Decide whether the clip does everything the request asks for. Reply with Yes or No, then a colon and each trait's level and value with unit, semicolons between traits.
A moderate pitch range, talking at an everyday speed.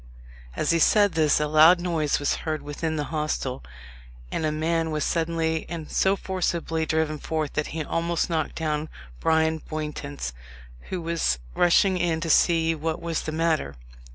No: narrow, 1.6 semitones; average, 165 wpm